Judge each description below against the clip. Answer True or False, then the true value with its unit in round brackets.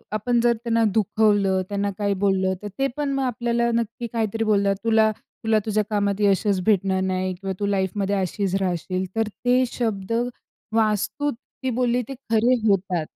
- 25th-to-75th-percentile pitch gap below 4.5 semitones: True (2.8 semitones)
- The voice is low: False (210 Hz)